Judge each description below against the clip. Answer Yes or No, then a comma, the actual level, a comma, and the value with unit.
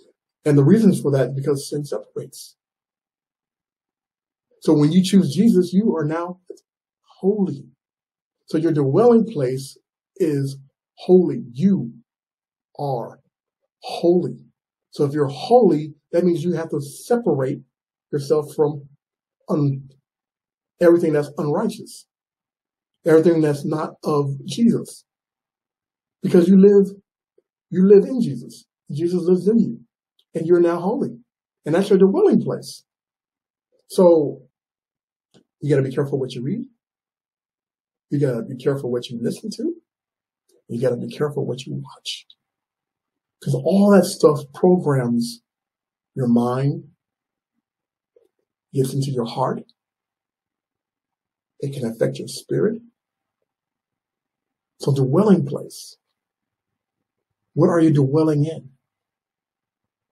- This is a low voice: No, medium, 160 Hz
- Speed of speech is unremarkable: No, slow, 120 wpm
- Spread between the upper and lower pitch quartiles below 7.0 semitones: Yes, wide, 5.5 semitones